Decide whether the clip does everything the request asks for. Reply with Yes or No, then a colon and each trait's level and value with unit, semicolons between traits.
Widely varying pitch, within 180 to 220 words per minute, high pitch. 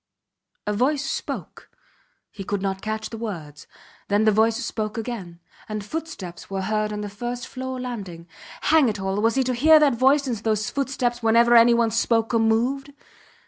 No: average, 3.3 semitones; average, 185 wpm; high, 225 Hz